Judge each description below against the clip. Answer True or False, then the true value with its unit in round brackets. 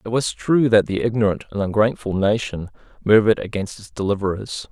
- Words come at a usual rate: True (165 wpm)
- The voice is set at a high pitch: False (105 Hz)